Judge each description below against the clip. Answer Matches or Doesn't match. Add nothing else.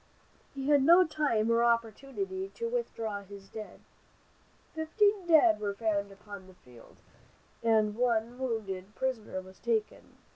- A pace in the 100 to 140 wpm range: Matches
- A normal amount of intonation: Doesn't match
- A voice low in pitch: Doesn't match